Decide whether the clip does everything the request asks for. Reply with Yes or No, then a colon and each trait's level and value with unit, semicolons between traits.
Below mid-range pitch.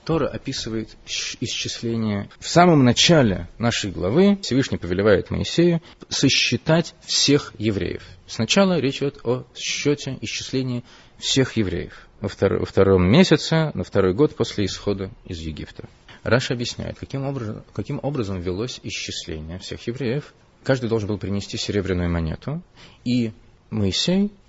Yes: low, 115 Hz